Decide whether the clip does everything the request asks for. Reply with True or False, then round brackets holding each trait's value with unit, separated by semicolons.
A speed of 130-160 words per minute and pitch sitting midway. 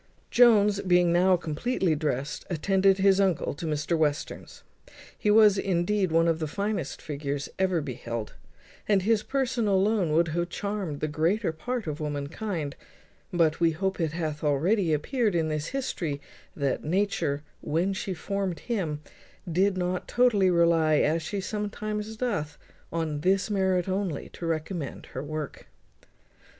True (145 wpm; 175 Hz)